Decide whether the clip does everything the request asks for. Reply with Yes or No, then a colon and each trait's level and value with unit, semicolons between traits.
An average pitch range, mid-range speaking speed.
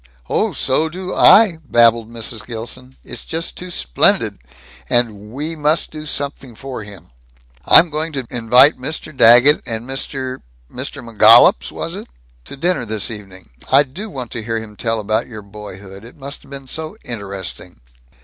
Yes: average, 4.9 semitones; average, 165 wpm